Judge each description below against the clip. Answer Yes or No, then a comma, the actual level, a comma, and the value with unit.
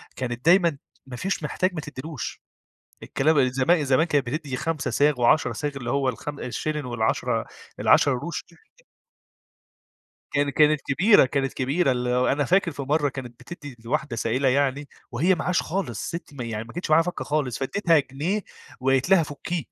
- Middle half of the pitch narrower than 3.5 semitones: No, average, 3.8 semitones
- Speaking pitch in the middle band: Yes, medium, 145 Hz